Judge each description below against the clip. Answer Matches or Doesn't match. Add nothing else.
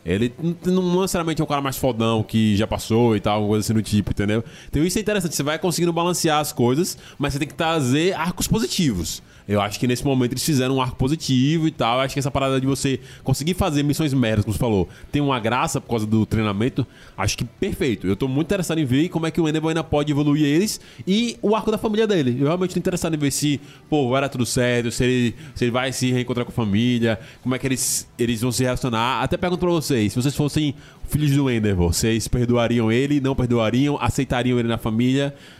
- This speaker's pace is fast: Matches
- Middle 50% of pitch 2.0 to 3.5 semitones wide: Doesn't match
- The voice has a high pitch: Doesn't match